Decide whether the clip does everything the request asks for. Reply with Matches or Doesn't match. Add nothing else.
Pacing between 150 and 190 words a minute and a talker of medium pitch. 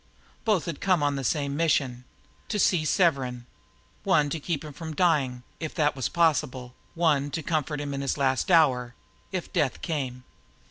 Matches